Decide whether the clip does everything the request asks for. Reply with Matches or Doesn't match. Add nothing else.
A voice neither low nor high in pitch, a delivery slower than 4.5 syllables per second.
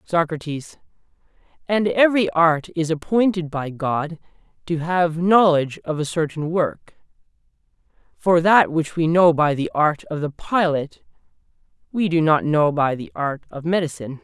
Doesn't match